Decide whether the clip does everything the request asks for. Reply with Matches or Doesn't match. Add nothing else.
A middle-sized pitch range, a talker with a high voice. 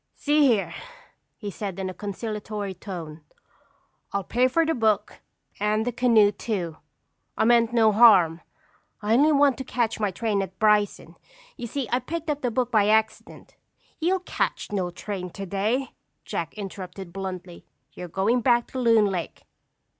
Matches